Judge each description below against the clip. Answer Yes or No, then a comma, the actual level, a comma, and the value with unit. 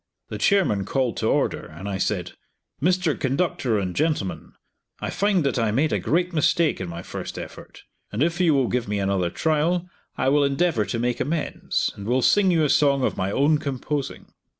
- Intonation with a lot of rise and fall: Yes, wide, 7.5 semitones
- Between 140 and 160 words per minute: No, average, 195 wpm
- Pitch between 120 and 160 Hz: Yes, medium, 140 Hz